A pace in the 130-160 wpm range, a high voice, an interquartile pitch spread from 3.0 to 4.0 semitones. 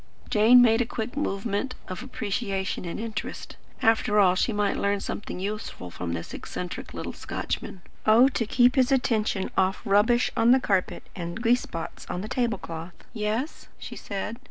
No: average, 170 wpm; high, 215 Hz; average, 3.7 semitones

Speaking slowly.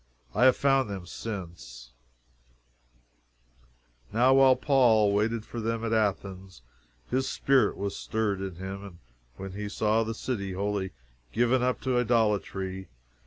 Yes: slow, 130 wpm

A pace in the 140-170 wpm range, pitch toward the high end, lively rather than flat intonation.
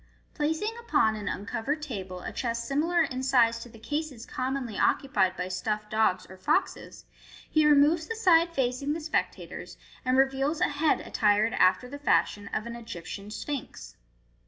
Yes: average, 165 wpm; very high, 255 Hz; wide, 5.7 semitones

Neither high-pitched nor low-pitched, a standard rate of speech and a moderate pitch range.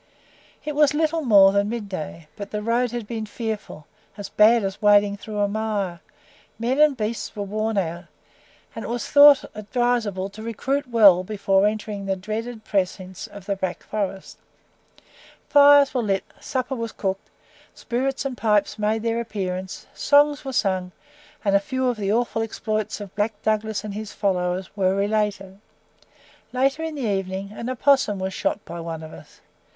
No: high, 215 Hz; average, 170 wpm; average, 3.4 semitones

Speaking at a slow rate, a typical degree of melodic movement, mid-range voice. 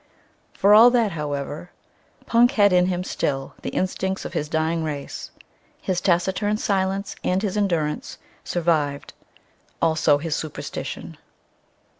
Yes: slow, 125 wpm; average, 4.3 semitones; medium, 180 Hz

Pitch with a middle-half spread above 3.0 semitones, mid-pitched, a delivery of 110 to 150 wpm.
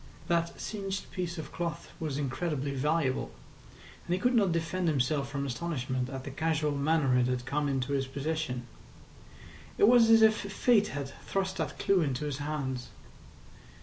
No: average, 4.6 semitones; medium, 150 Hz; average, 165 wpm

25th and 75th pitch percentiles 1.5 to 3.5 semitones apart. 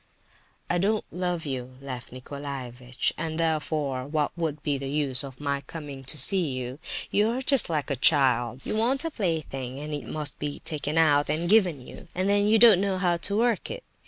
No: average, 5.1 semitones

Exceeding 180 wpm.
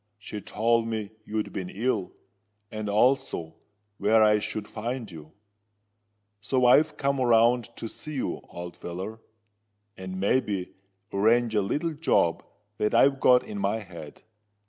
No: average, 140 wpm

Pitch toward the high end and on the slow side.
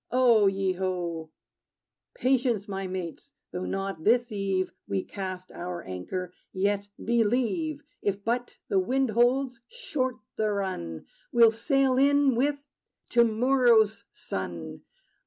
Yes: high, 215 Hz; slow, 125 wpm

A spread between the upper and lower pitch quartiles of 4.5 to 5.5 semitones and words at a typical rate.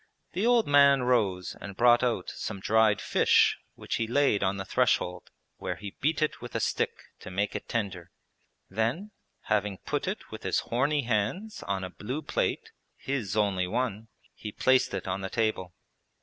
Yes: average, 5.0 semitones; average, 180 wpm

